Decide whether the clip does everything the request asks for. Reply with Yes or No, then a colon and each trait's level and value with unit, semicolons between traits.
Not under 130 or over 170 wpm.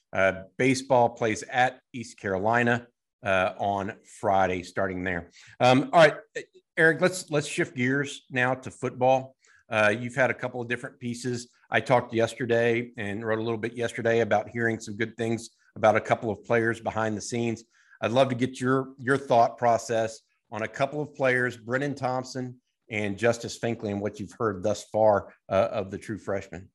No: average, 180 wpm